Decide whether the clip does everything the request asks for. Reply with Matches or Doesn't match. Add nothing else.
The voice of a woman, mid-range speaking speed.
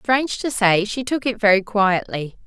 Matches